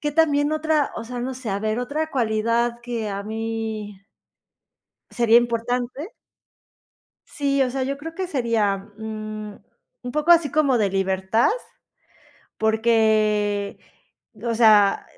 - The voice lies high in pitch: Yes, high, 230 Hz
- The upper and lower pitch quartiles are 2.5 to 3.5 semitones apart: No, average, 4.2 semitones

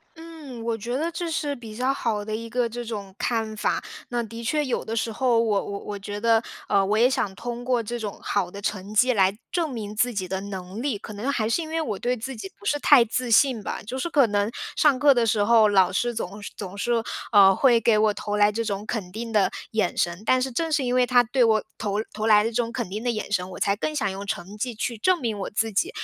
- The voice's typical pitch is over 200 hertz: Yes, high, 225 Hz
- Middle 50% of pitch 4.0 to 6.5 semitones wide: No, average, 3.3 semitones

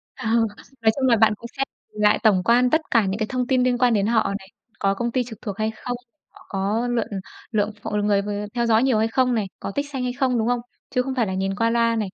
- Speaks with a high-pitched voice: Yes, high, 230 Hz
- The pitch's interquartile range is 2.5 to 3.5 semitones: Yes, average, 2.9 semitones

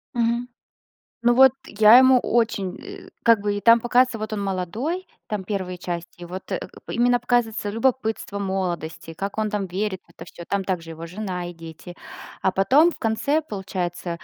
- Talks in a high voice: Yes, high, 205 Hz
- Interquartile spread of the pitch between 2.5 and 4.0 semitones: No, average, 4.6 semitones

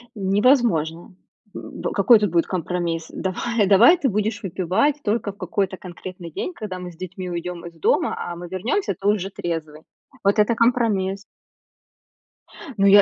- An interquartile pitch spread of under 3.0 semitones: No, average, 3.4 semitones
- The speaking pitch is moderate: No, high, 195 Hz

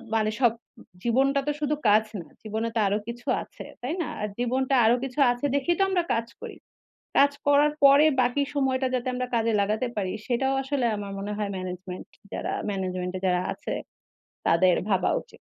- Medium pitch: No, high, 240 Hz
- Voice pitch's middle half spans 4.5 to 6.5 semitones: Yes, average, 4.8 semitones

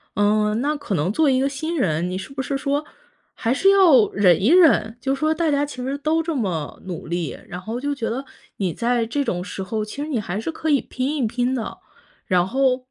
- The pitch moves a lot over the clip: Yes, wide, 5.8 semitones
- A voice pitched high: Yes, very high, 255 Hz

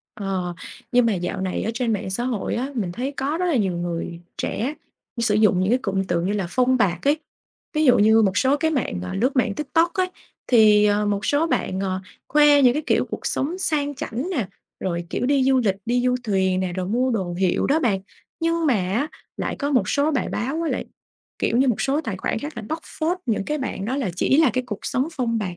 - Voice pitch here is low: No, high, 235 Hz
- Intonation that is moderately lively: No, wide, 6.5 semitones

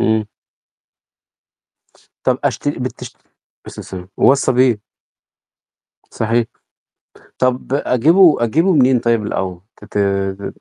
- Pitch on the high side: No, low, 120 Hz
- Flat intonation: No, average, 4.2 semitones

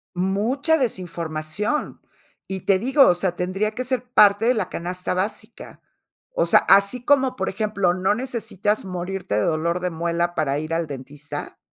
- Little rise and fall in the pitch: No, average, 4.2 semitones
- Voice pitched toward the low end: No, high, 190 Hz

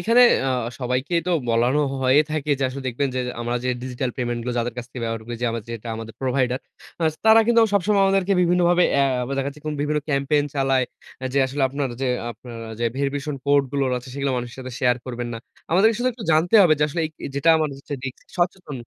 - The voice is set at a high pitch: No, medium, 140 Hz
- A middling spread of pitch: Yes, average, 4.3 semitones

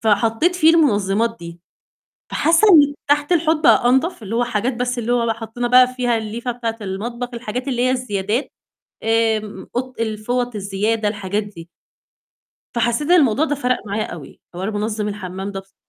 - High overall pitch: Yes, high, 230 Hz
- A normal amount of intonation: Yes, average, 3.4 semitones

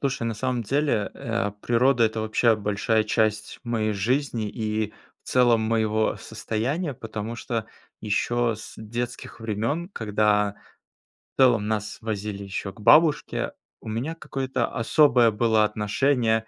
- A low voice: Yes, low, 115 Hz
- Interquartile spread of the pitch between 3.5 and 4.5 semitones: No, narrow, 2.4 semitones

